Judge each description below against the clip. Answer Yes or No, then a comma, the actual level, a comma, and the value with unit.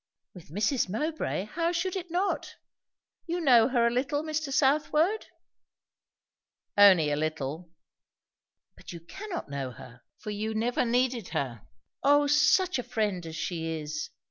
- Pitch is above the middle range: Yes, high, 235 Hz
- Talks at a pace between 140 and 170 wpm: Yes, average, 145 wpm